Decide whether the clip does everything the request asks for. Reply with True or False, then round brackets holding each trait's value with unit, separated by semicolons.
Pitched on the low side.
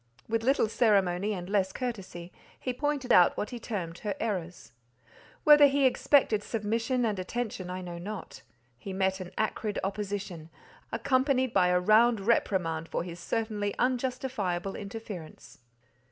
False (205 Hz)